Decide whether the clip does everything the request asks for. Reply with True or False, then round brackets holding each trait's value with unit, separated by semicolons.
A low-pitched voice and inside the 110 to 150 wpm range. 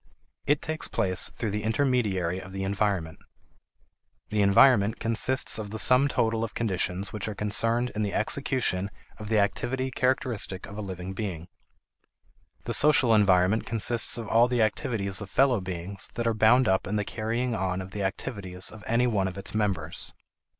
False (105 Hz; 175 wpm)